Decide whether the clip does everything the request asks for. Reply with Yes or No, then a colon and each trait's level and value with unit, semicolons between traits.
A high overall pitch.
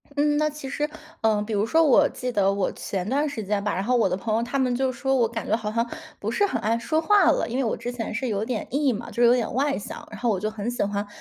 Yes: high, 235 Hz